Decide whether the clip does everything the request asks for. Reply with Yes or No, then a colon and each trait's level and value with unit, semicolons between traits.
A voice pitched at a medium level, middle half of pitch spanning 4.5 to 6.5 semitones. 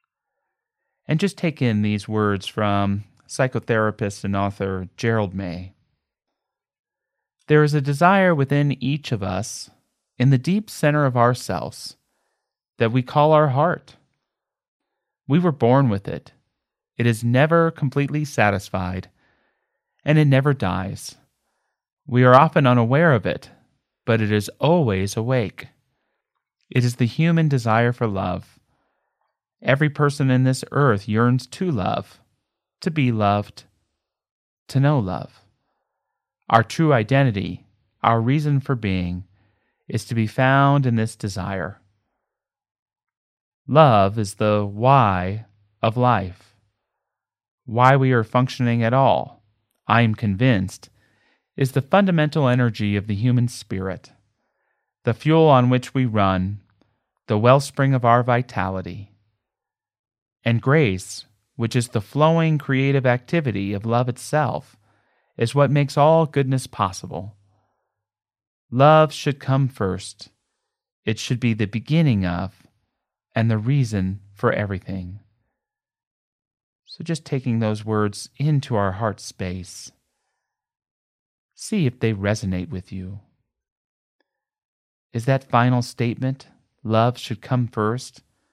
No: low, 120 Hz; average, 4.9 semitones